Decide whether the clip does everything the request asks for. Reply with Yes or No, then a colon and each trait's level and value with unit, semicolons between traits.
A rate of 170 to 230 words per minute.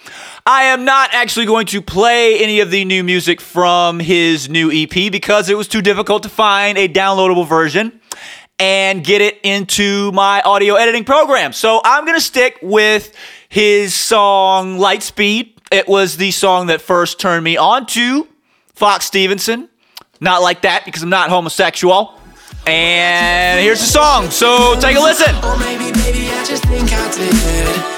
No: average, 150 wpm